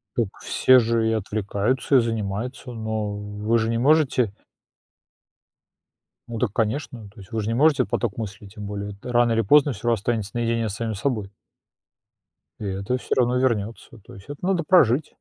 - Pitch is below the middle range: Yes, low, 115 Hz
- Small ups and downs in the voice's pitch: No, average, 3.3 semitones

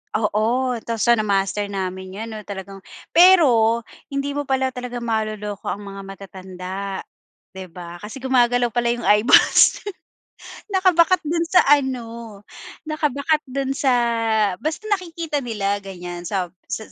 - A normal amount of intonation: No, wide, 5.8 semitones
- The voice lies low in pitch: No, high, 230 Hz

